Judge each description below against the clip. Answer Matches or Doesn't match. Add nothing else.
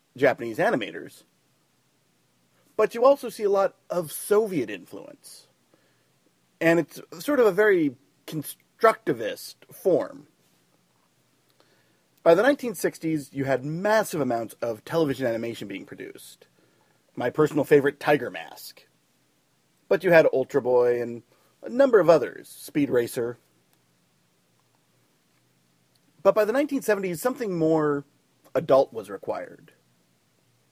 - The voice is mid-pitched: Matches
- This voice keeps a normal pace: Doesn't match